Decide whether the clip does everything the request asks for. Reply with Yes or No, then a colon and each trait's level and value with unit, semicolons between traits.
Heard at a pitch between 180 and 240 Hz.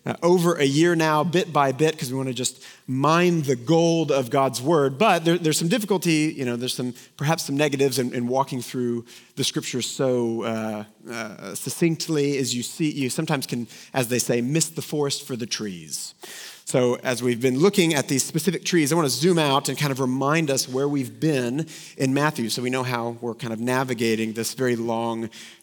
No: low, 135 Hz